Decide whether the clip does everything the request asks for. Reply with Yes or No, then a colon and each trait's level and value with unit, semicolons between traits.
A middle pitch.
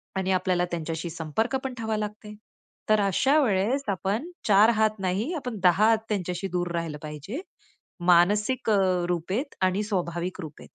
No: high, 195 Hz